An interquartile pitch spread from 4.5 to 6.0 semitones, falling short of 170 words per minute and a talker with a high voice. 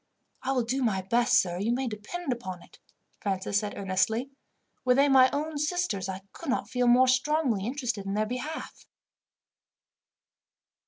Yes: average, 4.8 semitones; average, 160 wpm; high, 245 Hz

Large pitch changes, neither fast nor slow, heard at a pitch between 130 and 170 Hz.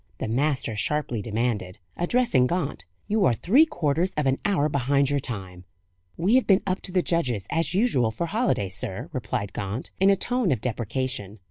Yes: wide, 8.3 semitones; average, 180 wpm; medium, 140 Hz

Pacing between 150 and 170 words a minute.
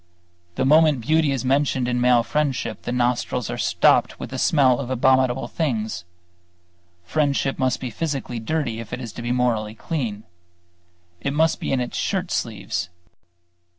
Yes: average, 160 wpm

